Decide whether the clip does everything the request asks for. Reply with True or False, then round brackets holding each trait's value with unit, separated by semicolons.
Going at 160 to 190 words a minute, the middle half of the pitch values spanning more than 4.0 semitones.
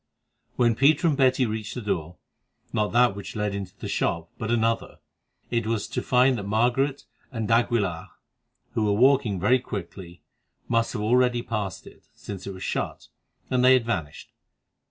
False (170 wpm; 3.7 semitones)